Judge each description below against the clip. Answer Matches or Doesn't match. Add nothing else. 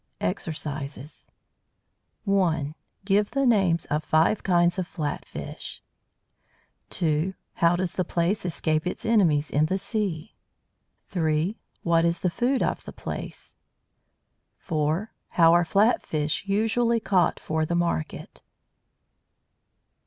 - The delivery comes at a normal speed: Doesn't match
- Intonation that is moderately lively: Matches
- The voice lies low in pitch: Doesn't match